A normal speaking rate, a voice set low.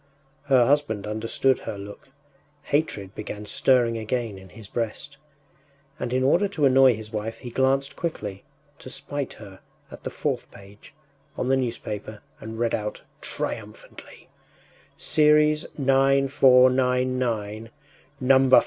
No: slow, 130 wpm; low, 125 Hz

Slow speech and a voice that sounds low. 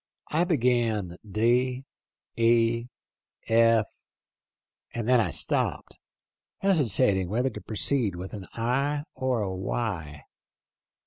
Yes: slow, 125 wpm; low, 115 Hz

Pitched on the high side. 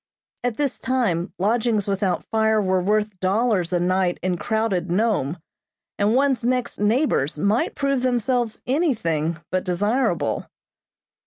Yes: high, 210 Hz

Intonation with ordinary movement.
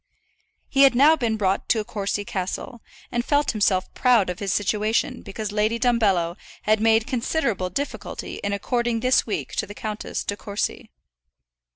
Yes: average, 3.0 semitones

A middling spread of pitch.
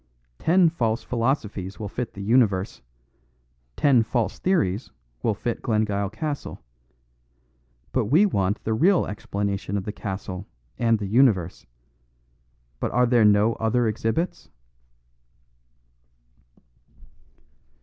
Yes: average, 3.7 semitones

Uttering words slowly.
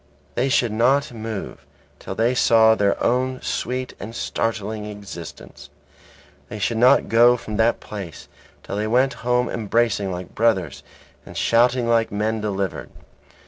No: average, 145 wpm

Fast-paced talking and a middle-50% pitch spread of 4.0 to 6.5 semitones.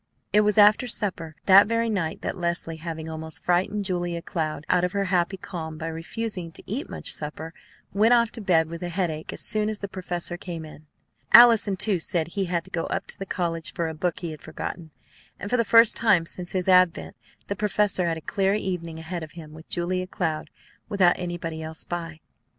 No: fast, 215 wpm; average, 3.6 semitones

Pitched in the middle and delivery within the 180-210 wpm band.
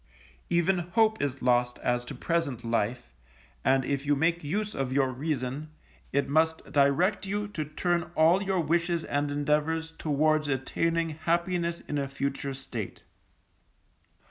No: medium, 150 Hz; average, 145 wpm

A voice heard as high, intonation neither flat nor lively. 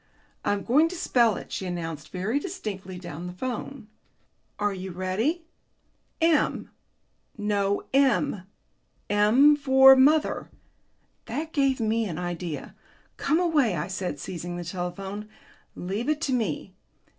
No: high, 210 Hz; wide, 7.1 semitones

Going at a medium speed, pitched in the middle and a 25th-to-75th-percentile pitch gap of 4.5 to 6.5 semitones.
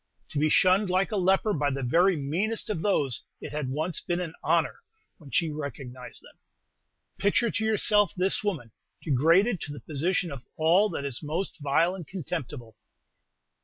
Yes: average, 170 wpm; medium, 165 Hz; average, 5.1 semitones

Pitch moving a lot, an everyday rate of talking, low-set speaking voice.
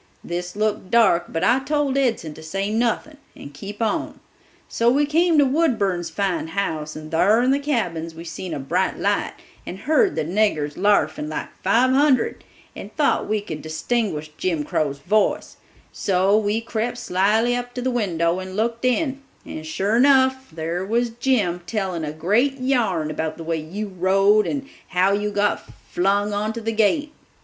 No: wide, 6.1 semitones; average, 175 wpm; high, 205 Hz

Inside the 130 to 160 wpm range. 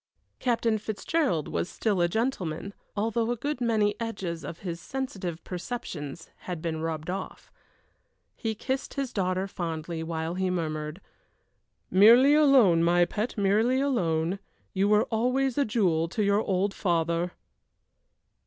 Yes: average, 145 wpm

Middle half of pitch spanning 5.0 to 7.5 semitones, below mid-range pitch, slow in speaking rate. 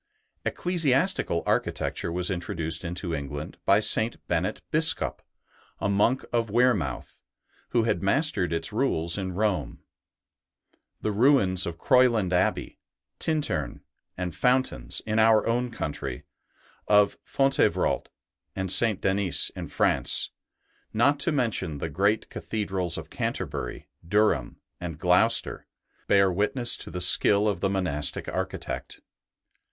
Yes: average, 5.3 semitones; low, 100 Hz; slow, 120 wpm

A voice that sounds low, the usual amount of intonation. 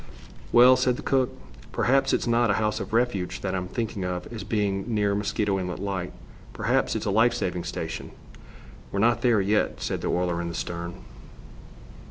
Yes: low, 100 Hz; average, 4.4 semitones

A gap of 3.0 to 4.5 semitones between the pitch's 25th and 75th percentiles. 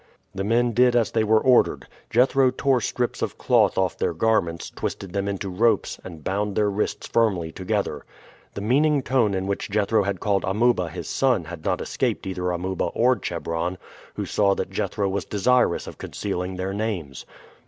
Yes: average, 4.0 semitones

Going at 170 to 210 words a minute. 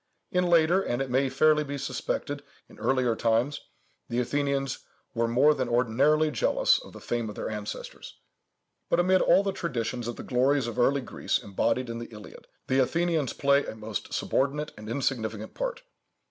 Yes: average, 175 wpm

